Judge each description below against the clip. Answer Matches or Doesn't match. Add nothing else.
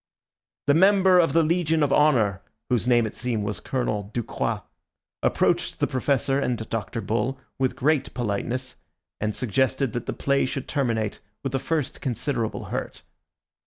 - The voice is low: Matches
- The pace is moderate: Matches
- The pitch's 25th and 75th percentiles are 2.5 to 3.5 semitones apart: Doesn't match